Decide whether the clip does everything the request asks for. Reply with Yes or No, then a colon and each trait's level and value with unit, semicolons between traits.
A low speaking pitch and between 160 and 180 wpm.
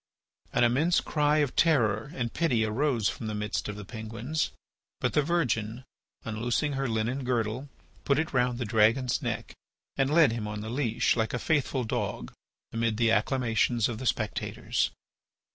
Yes: low, 120 Hz; average, 165 wpm